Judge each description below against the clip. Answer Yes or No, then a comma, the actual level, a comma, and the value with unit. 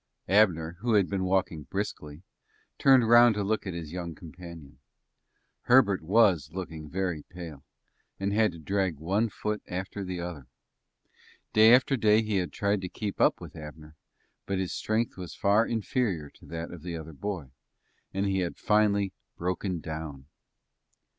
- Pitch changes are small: No, average, 4.2 semitones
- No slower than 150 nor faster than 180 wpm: Yes, average, 160 wpm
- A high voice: No, very low, 95 Hz